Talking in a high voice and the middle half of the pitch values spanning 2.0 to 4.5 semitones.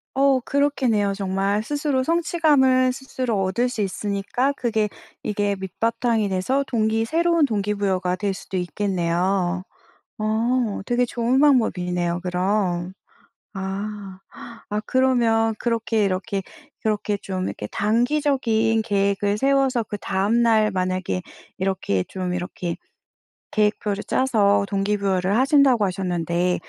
Yes: high, 210 Hz; average, 4.2 semitones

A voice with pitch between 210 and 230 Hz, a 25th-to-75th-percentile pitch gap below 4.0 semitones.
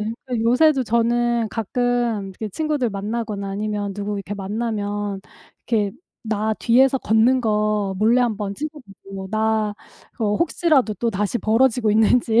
Yes: high, 220 Hz; narrow, 2.6 semitones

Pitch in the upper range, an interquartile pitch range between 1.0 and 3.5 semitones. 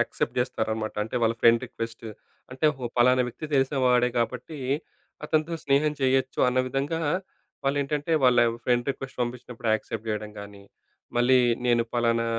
No: low, 125 Hz; narrow, 2.6 semitones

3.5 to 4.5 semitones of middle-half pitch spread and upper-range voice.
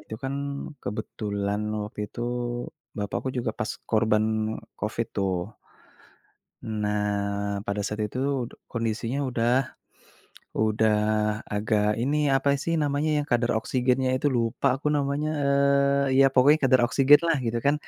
No: average, 4.1 semitones; low, 115 Hz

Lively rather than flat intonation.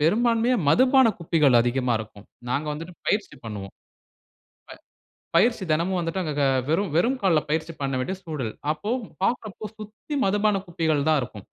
Yes: wide, 6.6 semitones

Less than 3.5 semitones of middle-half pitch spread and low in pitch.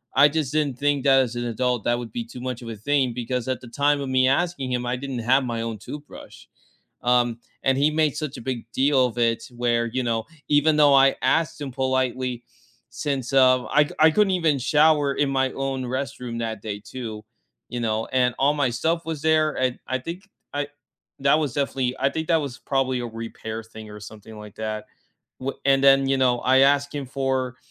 Yes: average, 2.8 semitones; low, 130 Hz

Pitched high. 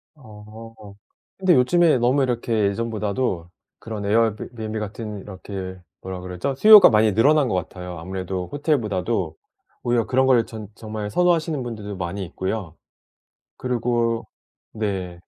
No: low, 110 Hz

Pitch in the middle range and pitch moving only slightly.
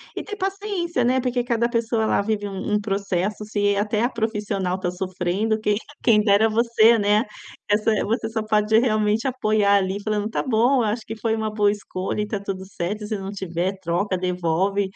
No: high, 210 Hz; narrow, 2.2 semitones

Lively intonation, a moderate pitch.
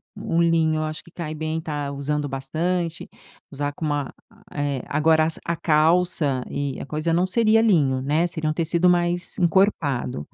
No: average, 2.9 semitones; medium, 155 Hz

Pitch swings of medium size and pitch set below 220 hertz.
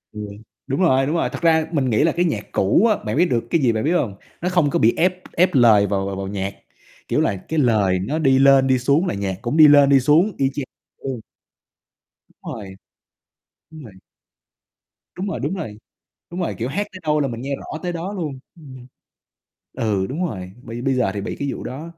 No: wide, 6.4 semitones; low, 135 Hz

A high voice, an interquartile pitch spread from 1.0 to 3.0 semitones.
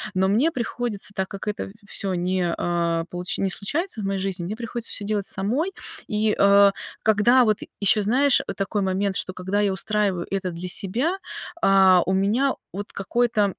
Yes: high, 200 Hz; narrow, 2.6 semitones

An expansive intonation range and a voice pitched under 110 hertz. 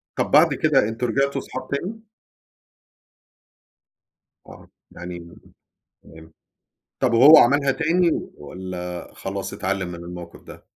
Yes: wide, 7.8 semitones; low, 100 Hz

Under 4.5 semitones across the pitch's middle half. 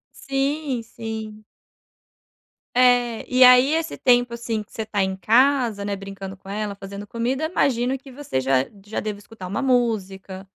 Yes: average, 4.1 semitones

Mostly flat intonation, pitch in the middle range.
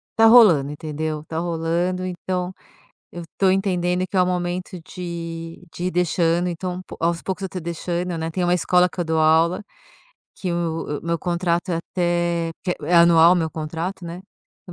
Yes: narrow, 1.6 semitones; medium, 175 Hz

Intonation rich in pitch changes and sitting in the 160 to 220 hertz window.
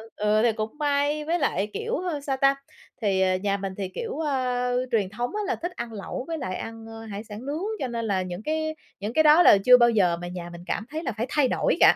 No: wide, 6.5 semitones; high, 240 Hz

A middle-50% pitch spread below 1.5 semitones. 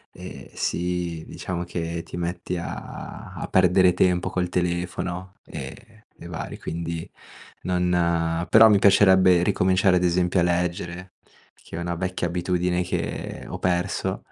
Yes: narrow, 1.1 semitones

